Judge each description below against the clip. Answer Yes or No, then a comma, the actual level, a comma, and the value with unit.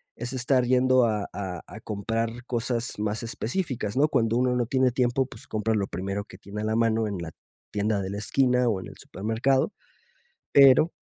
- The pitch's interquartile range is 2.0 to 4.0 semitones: Yes, average, 3.3 semitones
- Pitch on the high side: No, low, 115 Hz